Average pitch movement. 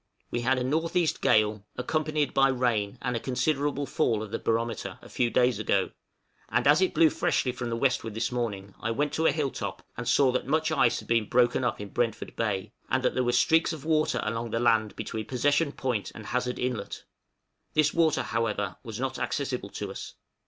Yes: average, 3.9 semitones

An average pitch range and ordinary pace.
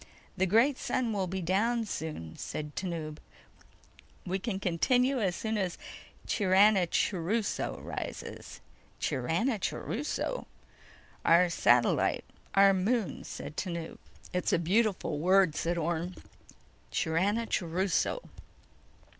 No: average, 4.3 semitones; slow, 95 wpm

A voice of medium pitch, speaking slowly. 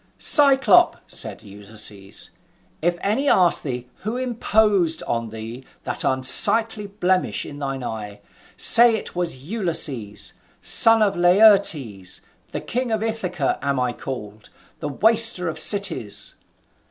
Yes: medium, 175 Hz; slow, 125 wpm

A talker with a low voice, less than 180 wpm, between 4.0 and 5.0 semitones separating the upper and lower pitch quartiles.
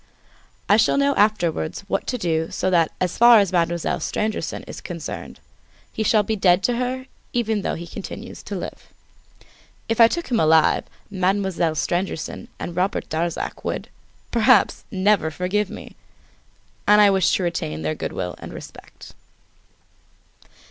No: high, 190 Hz; average, 155 wpm; average, 4.3 semitones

